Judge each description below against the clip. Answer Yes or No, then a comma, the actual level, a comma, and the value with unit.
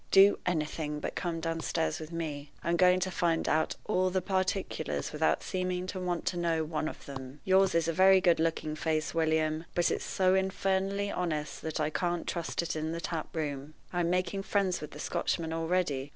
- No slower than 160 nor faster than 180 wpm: No, average, 195 wpm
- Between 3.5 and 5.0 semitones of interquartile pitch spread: No, average, 2.8 semitones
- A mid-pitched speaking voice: Yes, medium, 170 Hz